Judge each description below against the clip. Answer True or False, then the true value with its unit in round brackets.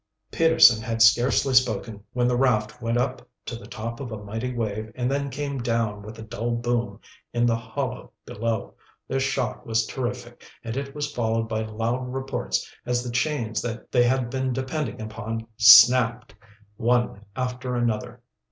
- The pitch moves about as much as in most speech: False (2.1 semitones)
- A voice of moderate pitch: False (120 Hz)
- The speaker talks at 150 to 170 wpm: True (165 wpm)